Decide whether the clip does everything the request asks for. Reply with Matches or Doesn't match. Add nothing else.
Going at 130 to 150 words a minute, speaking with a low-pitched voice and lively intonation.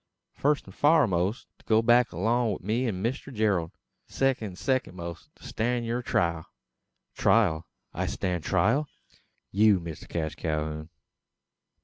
Matches